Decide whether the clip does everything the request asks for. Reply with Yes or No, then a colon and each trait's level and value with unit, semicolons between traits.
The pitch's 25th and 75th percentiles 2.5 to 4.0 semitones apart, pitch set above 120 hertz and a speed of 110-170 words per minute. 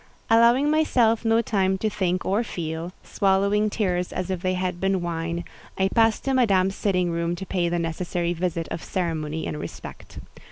Yes: average, 3.5 semitones; medium, 185 Hz; average, 165 wpm